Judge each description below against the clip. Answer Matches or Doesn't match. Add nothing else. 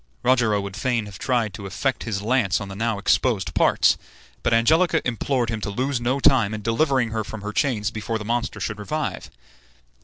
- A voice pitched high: Doesn't match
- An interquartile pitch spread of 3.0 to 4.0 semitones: Matches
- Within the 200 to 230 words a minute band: Matches